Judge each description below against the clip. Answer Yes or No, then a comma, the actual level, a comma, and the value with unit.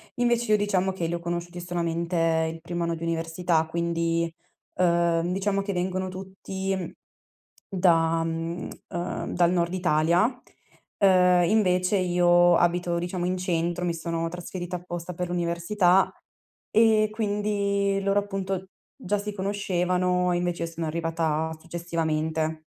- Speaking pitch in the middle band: Yes, medium, 175 Hz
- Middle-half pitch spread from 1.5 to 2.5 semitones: Yes, narrow, 2.2 semitones